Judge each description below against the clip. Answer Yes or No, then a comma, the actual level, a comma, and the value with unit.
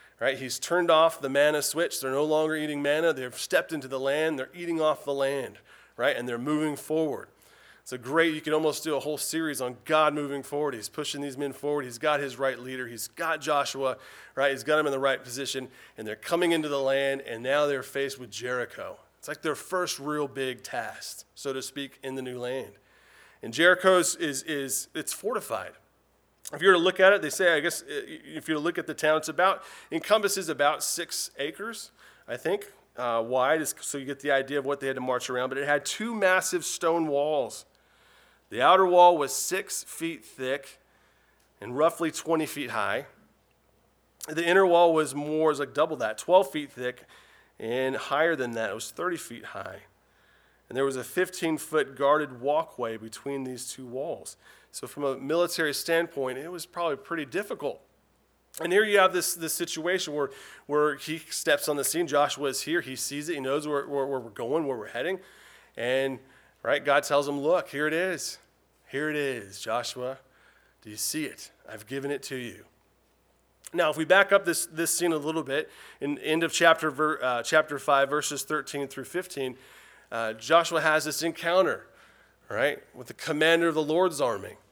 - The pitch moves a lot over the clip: No, average, 3.5 semitones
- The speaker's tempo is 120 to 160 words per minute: No, fast, 205 wpm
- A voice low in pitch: No, medium, 150 Hz